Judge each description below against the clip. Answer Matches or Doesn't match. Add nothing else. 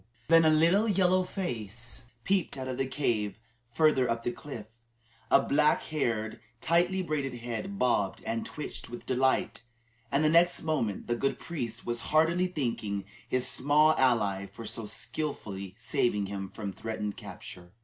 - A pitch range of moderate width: Doesn't match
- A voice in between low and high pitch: Doesn't match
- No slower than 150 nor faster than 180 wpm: Matches